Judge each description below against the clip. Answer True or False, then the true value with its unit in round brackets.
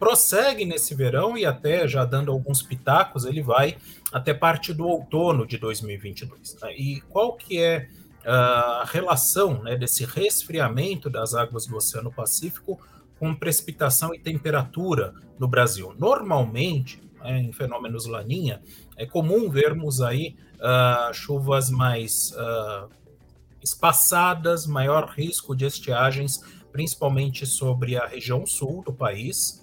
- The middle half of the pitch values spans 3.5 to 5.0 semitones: True (4.7 semitones)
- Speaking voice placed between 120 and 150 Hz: True (135 Hz)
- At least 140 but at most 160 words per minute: False (130 wpm)